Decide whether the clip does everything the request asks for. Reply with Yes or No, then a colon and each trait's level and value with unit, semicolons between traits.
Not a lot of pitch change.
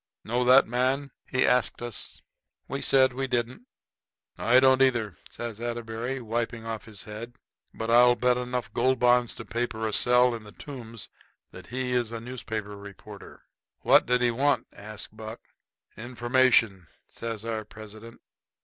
Yes: narrow, 2.1 semitones